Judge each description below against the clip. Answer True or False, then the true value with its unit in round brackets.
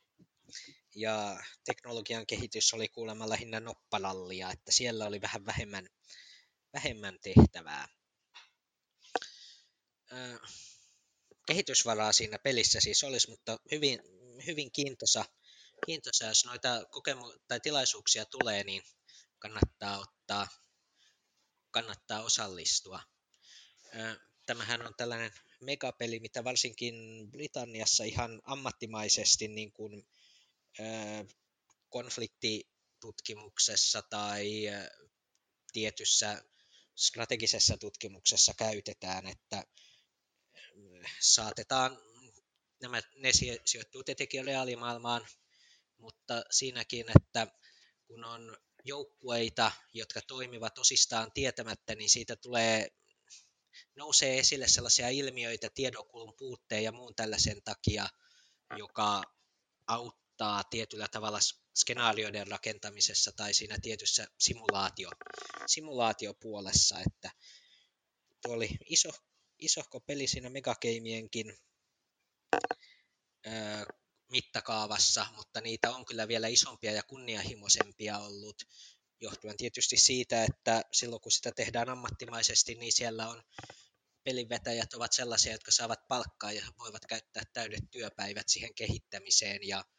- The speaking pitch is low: True (115 Hz)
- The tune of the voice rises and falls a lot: False (2.4 semitones)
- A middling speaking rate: False (90 wpm)